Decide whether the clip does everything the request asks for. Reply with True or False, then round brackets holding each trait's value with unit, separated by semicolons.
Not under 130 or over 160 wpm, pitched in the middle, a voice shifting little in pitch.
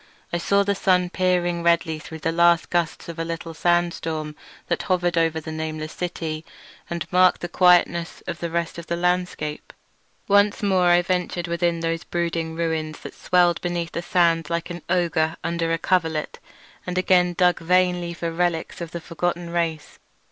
False (175 wpm; 170 Hz; 1.3 semitones)